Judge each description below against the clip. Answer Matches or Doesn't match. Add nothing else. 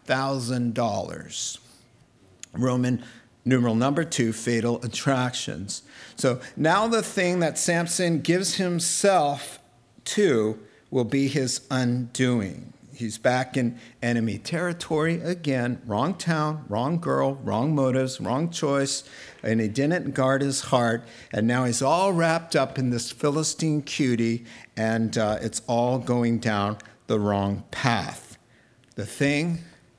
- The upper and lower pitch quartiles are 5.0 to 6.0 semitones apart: Doesn't match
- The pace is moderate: Doesn't match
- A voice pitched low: Matches